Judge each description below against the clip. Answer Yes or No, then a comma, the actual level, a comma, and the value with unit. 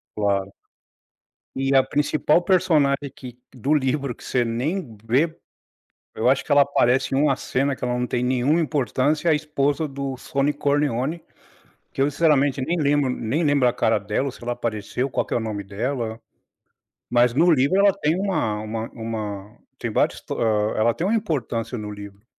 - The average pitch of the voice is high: No, low, 135 Hz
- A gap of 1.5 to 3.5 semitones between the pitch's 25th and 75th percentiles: No, average, 4.3 semitones